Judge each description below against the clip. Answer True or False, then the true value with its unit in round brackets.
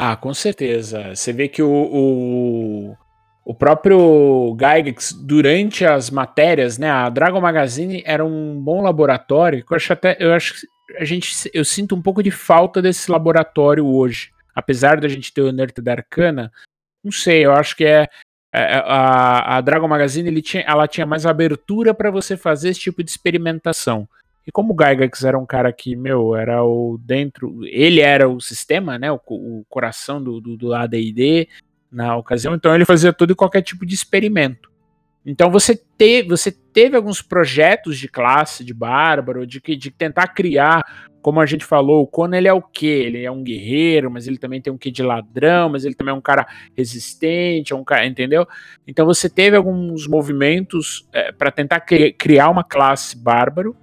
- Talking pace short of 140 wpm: False (180 wpm)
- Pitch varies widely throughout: False (4.9 semitones)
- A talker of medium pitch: True (150 Hz)